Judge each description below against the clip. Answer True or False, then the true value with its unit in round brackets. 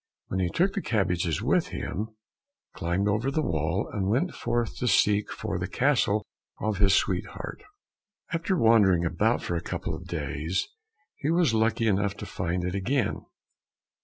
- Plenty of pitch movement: False (4.4 semitones)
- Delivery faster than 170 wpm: False (160 wpm)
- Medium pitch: False (100 Hz)